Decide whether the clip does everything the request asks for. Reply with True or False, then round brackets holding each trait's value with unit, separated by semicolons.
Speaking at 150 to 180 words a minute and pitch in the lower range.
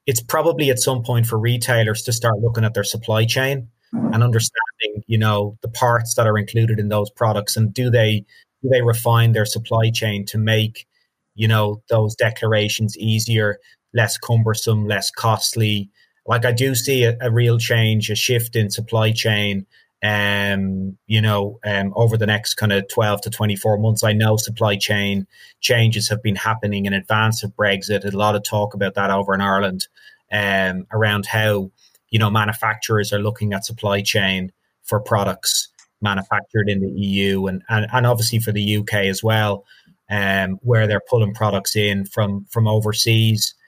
True (175 wpm; 110 Hz)